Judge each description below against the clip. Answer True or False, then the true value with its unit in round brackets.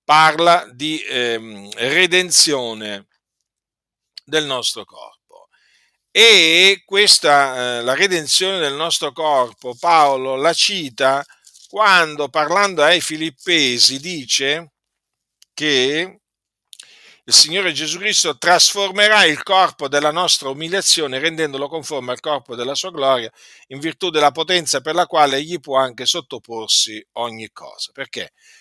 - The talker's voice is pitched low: False (155 Hz)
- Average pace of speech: False (110 wpm)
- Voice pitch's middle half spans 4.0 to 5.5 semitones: True (5.2 semitones)